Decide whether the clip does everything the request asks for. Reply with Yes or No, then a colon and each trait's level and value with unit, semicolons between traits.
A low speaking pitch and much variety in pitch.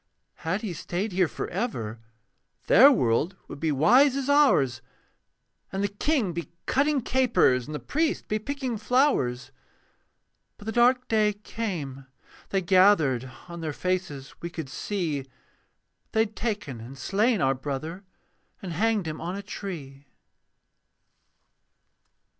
No: medium, 185 Hz; wide, 7.7 semitones